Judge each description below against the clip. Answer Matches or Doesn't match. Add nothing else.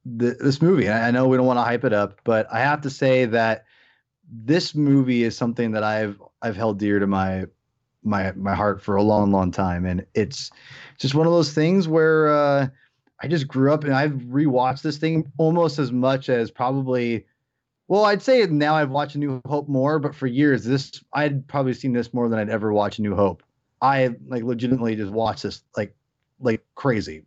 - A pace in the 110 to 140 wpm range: Doesn't match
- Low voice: Matches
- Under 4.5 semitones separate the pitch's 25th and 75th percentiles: Doesn't match